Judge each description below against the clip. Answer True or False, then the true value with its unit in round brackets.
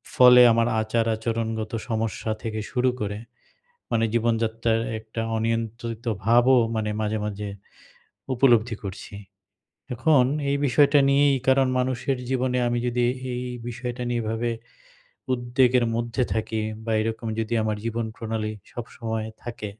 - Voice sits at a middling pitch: False (115 Hz)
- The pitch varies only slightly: True (1.9 semitones)